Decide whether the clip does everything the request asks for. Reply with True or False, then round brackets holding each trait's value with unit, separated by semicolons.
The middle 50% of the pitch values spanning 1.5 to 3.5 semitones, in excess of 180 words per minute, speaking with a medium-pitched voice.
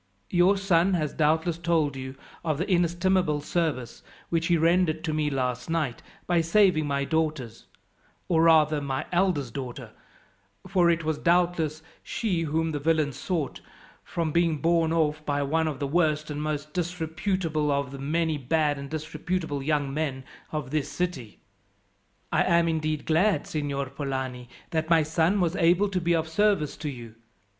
False (2.8 semitones; 165 wpm; 160 Hz)